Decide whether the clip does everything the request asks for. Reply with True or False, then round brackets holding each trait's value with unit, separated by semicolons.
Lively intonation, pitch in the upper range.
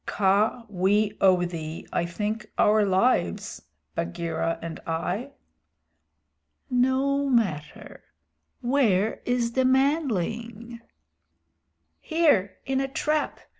True (6.2 semitones; 215 Hz)